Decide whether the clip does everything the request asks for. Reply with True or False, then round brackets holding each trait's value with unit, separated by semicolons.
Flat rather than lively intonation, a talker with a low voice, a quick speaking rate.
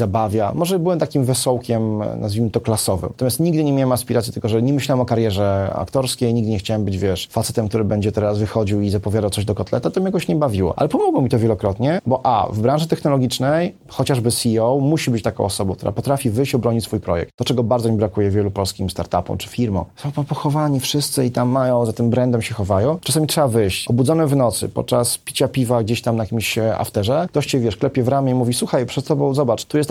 False (4.3 semitones; 120 Hz; 225 wpm)